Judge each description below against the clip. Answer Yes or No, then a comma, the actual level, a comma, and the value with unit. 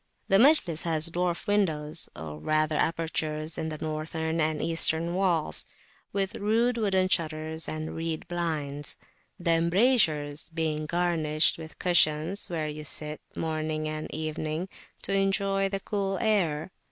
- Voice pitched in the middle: Yes, medium, 160 Hz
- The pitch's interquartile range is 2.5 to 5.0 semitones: Yes, average, 3.4 semitones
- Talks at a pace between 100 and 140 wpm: Yes, slow, 135 wpm